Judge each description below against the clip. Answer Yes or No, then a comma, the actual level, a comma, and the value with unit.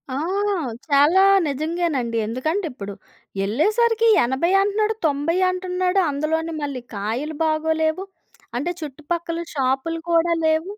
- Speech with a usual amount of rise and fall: Yes, average, 4.1 semitones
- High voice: Yes, very high, 315 Hz